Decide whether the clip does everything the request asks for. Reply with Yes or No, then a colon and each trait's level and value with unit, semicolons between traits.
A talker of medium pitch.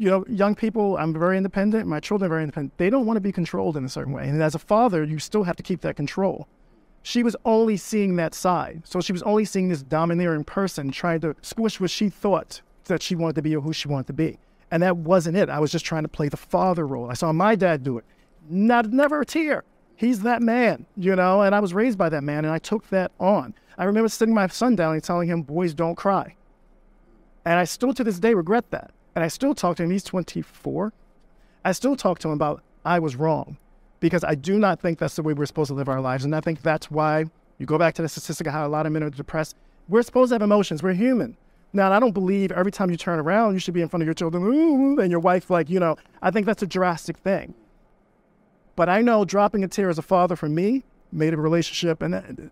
Yes: medium, 180 Hz